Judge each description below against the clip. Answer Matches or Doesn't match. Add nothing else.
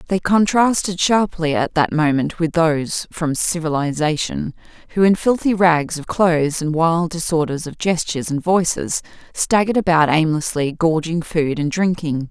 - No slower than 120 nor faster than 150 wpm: Matches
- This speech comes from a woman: Matches